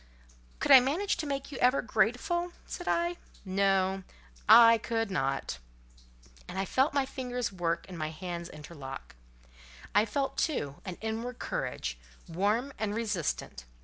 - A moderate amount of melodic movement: No, wide, 6.9 semitones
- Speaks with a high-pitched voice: Yes, high, 220 Hz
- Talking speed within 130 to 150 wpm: Yes, average, 145 wpm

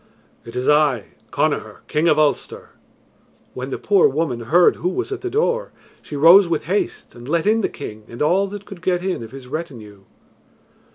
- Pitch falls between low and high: Yes, medium, 155 Hz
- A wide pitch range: Yes, wide, 6.8 semitones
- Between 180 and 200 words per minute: Yes, average, 190 wpm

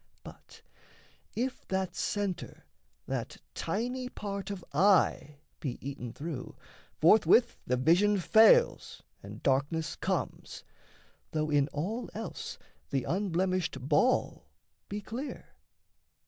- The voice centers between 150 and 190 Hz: Yes, medium, 185 Hz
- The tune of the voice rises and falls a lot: Yes, wide, 6.0 semitones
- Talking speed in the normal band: No, slow, 105 wpm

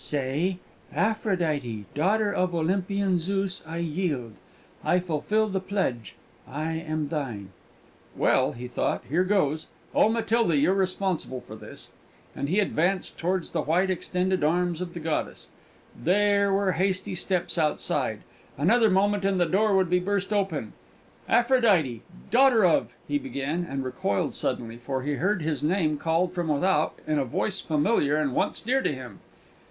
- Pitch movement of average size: Yes, average, 4.8 semitones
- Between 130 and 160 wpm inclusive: Yes, average, 155 wpm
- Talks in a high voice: No, medium, 175 Hz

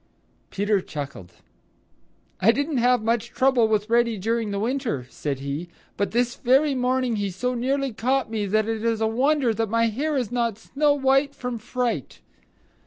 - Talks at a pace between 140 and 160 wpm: No, average, 175 wpm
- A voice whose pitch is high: Yes, high, 230 Hz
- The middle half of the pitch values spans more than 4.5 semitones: No, average, 3.4 semitones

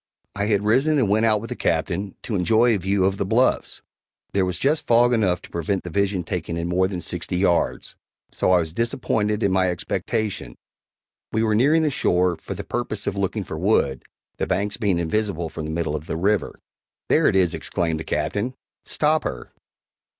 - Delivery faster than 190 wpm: Yes, average, 200 wpm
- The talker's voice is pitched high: No, low, 100 Hz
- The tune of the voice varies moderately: Yes, average, 4.0 semitones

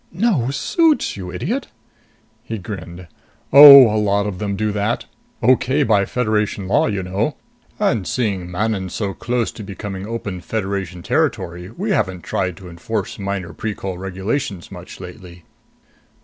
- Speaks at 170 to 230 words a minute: No, average, 145 wpm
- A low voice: Yes, low, 100 Hz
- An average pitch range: Yes, average, 3.7 semitones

